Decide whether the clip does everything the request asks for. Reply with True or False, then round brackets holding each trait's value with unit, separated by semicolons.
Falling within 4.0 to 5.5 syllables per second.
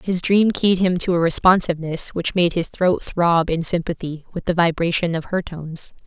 True (5.0 syllables/s)